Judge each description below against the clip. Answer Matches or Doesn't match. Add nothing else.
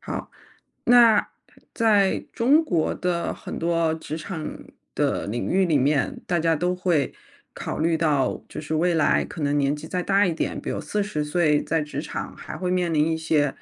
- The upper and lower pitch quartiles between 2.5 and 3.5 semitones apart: Matches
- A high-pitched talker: Doesn't match